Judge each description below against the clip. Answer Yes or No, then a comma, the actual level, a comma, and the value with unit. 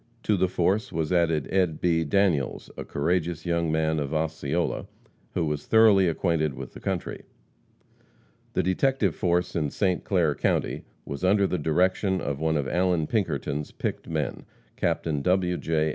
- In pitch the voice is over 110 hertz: No, very low, 85 Hz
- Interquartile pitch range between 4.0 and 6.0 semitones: No, average, 3.1 semitones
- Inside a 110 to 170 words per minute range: Yes, average, 160 wpm